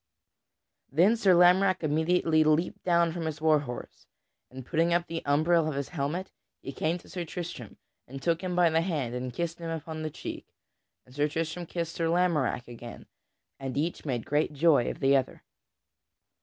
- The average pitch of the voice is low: No, medium, 160 Hz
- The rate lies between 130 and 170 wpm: No, average, 185 wpm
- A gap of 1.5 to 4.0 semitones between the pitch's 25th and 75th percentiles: Yes, average, 3.4 semitones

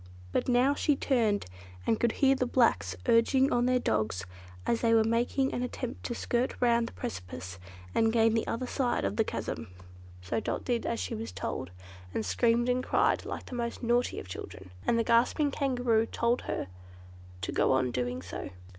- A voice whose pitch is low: No, high, 235 Hz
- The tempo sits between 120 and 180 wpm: No, average, 190 wpm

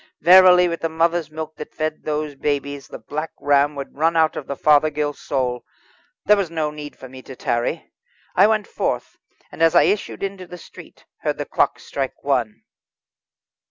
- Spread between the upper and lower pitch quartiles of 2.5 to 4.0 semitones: Yes, average, 2.9 semitones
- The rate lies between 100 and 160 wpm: No, average, 185 wpm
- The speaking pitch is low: No, medium, 155 Hz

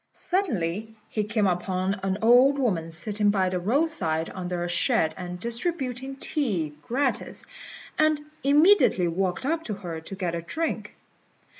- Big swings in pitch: Yes, wide, 7.3 semitones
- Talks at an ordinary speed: Yes, average, 145 wpm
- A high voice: Yes, high, 205 Hz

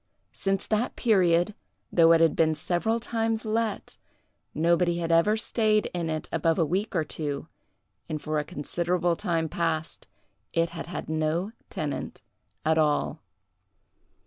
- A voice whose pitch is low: No, medium, 170 Hz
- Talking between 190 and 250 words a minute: No, average, 145 wpm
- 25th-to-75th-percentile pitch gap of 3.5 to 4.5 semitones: Yes, average, 3.8 semitones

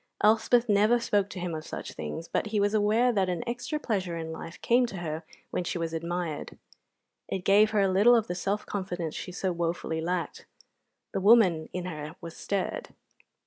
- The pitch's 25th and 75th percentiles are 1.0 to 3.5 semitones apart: No, average, 4.0 semitones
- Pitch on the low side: No, medium, 185 Hz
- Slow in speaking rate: No, average, 195 wpm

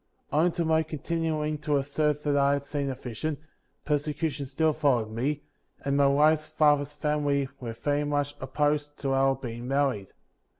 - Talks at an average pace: Yes, average, 170 wpm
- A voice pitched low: No, medium, 145 Hz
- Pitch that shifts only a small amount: Yes, narrow, 1.7 semitones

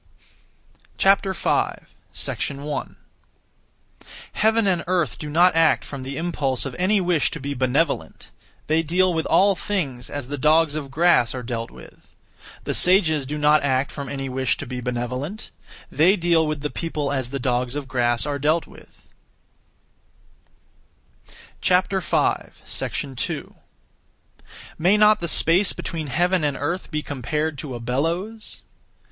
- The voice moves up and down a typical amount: Yes, average, 4.5 semitones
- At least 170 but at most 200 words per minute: No, average, 140 wpm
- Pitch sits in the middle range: Yes, medium, 150 Hz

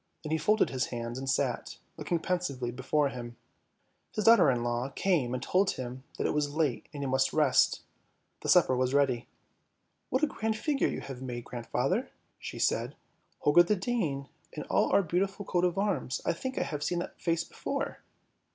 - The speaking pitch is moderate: Yes, medium, 145 Hz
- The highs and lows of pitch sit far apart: Yes, wide, 6.1 semitones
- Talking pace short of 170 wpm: No, average, 200 wpm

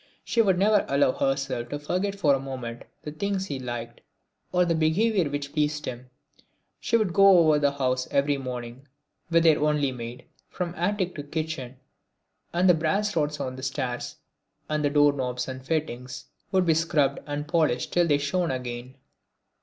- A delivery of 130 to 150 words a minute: No, average, 175 wpm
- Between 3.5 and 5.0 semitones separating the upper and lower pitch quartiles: Yes, average, 4.6 semitones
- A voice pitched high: No, medium, 145 Hz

